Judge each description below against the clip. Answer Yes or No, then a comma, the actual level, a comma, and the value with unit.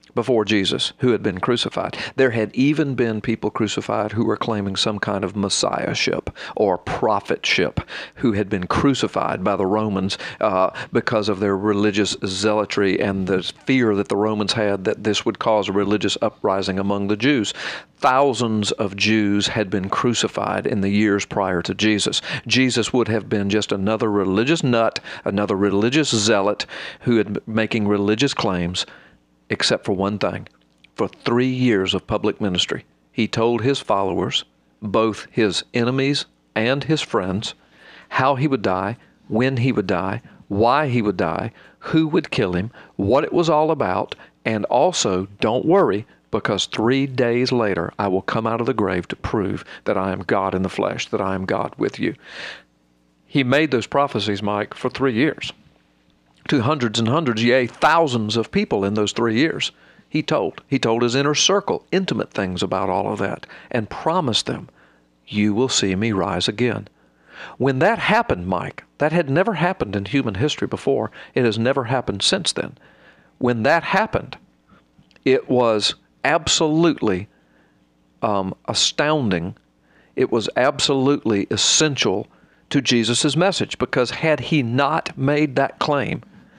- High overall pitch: No, low, 110 Hz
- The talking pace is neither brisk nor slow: Yes, average, 160 wpm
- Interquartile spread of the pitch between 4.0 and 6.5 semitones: Yes, average, 4.9 semitones